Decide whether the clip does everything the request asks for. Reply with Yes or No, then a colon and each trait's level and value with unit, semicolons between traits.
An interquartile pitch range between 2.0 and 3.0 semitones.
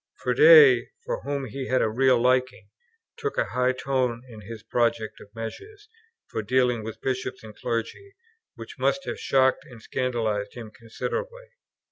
No: average, 3.7 semitones